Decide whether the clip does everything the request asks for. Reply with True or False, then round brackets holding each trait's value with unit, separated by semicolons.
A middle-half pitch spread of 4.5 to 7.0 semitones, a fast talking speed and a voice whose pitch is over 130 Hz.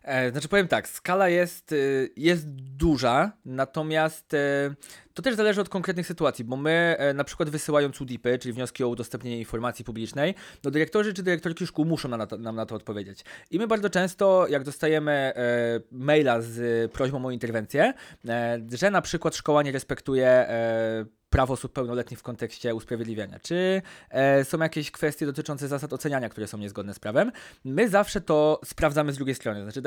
True (5.1 semitones; 165 wpm; 140 Hz)